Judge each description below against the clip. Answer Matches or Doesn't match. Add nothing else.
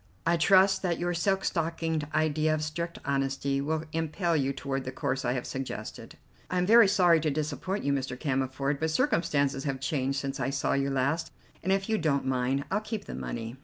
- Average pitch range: Matches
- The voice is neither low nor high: Matches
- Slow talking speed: Doesn't match